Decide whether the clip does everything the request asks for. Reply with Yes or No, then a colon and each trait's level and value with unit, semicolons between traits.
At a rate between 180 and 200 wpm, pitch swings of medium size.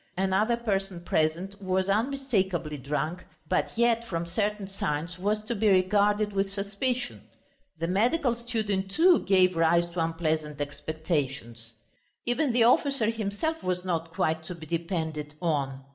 No: average, 140 wpm; average, 4.8 semitones